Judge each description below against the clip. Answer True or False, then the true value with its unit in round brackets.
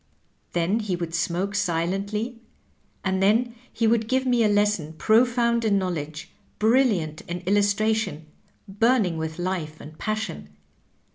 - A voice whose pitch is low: False (200 Hz)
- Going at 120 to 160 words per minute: True (140 wpm)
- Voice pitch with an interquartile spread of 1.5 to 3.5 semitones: False (4.5 semitones)